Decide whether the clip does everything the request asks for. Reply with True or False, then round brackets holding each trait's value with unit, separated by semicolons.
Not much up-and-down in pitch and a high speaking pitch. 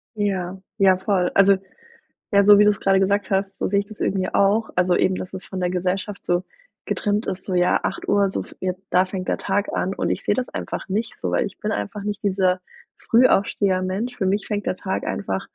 True (1.7 semitones; 195 Hz)